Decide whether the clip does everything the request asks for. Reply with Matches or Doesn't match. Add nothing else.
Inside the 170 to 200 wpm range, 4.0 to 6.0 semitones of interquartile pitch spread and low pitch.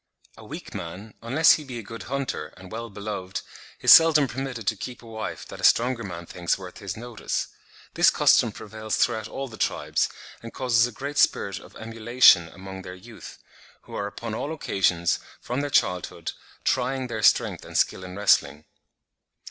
Matches